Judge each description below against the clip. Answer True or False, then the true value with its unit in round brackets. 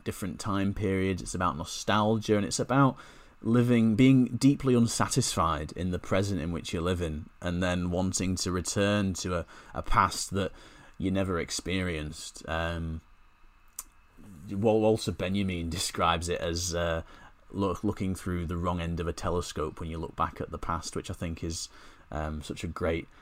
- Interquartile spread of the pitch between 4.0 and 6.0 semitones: False (3.5 semitones)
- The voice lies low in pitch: True (90 Hz)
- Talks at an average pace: True (165 wpm)